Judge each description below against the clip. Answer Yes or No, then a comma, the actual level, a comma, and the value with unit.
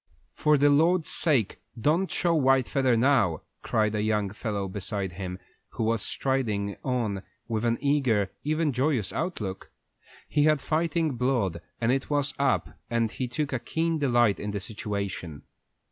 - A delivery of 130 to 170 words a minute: Yes, average, 160 wpm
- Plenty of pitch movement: Yes, wide, 5.8 semitones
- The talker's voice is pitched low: Yes, low, 120 Hz